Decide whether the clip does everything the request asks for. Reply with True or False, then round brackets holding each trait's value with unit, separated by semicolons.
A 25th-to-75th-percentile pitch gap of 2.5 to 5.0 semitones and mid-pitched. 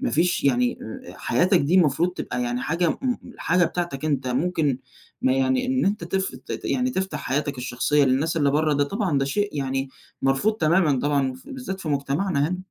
False (5.5 semitones; 155 Hz)